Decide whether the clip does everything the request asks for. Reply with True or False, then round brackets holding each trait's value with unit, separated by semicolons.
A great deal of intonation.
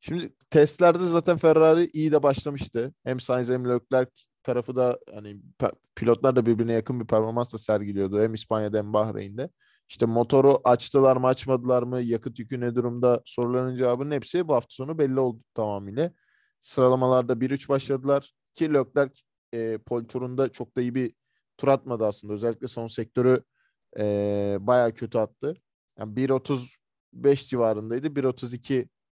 False (2.8 semitones)